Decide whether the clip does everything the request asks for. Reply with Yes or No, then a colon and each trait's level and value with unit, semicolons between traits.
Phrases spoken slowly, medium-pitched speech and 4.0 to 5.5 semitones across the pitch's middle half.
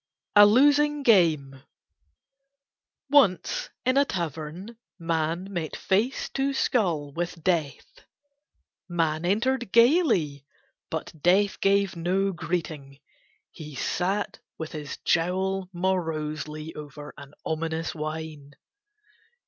Yes: slow, 100 wpm; medium, 175 Hz; average, 4.5 semitones